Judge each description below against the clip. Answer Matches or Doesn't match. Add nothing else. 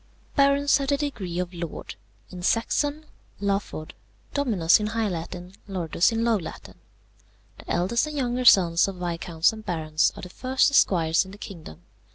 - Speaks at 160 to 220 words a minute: Matches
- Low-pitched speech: Doesn't match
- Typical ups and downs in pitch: Doesn't match